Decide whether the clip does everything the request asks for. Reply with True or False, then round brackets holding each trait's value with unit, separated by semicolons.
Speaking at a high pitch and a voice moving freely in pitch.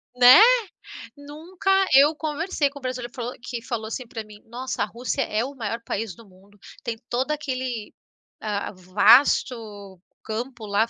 False (240 Hz; 3.8 semitones)